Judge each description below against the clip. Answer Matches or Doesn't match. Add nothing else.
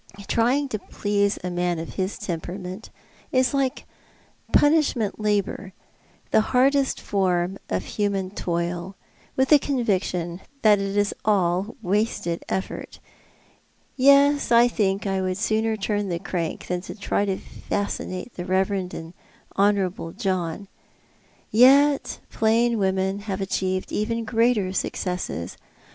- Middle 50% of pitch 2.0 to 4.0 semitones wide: Matches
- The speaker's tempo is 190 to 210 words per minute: Doesn't match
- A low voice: Doesn't match